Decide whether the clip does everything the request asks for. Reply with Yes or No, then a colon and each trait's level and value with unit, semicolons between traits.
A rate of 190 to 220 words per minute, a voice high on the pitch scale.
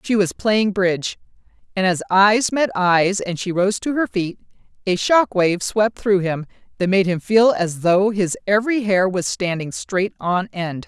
Yes: average, 195 wpm; high, 195 Hz